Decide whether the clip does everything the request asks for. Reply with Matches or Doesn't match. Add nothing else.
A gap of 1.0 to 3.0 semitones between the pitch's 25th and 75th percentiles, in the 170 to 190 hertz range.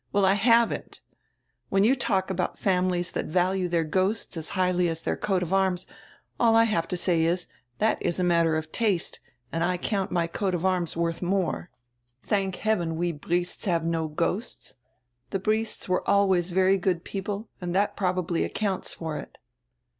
Matches